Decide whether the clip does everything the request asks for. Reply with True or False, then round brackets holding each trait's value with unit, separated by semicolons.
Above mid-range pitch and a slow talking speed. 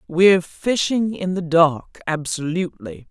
False (170 Hz; 115 wpm)